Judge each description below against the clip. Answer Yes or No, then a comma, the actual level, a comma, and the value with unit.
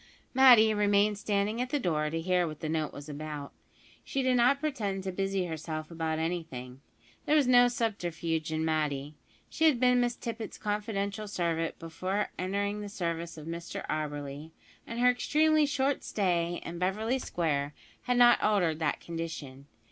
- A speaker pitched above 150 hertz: Yes, medium, 185 Hz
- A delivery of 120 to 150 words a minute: No, average, 165 wpm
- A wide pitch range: Yes, wide, 6.1 semitones